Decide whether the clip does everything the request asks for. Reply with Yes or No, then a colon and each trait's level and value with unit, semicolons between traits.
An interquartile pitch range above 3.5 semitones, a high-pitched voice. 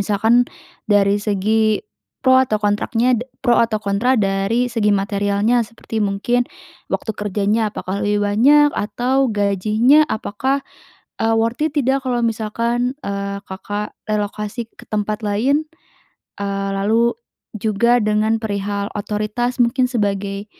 No: average, 3.0 semitones; high, 215 Hz